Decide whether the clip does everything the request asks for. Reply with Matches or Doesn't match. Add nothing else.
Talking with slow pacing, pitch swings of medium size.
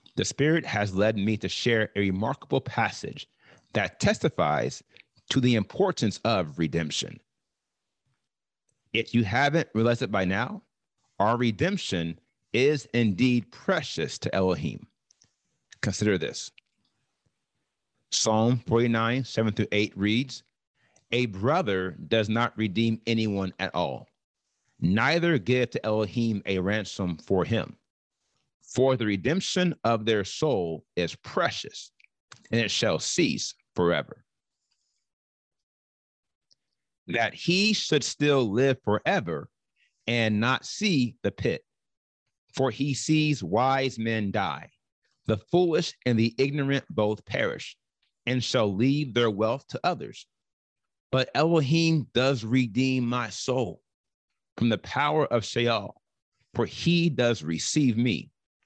Matches